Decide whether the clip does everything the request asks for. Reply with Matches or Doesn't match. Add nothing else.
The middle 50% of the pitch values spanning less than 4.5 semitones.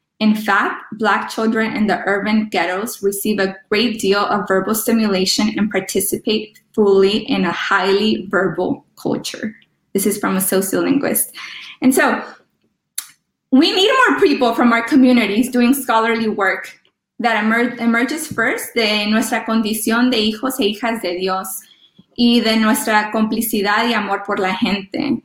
Matches